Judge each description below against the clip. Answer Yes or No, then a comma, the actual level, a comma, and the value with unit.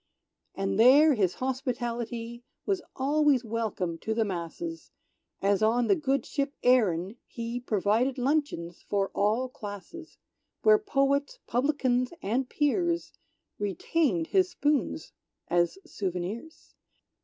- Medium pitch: No, high, 245 Hz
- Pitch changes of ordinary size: No, wide, 5.8 semitones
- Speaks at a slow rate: Yes, slow, 110 wpm